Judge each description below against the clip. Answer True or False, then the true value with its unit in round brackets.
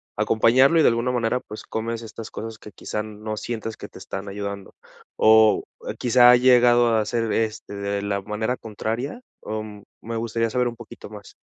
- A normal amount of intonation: False (2.1 semitones)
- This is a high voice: False (110 Hz)